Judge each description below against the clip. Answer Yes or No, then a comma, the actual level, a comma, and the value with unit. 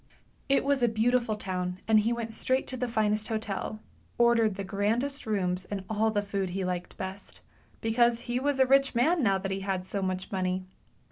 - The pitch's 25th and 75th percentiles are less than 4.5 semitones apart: Yes, average, 3.7 semitones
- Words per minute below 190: No, average, 200 wpm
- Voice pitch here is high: Yes, high, 215 Hz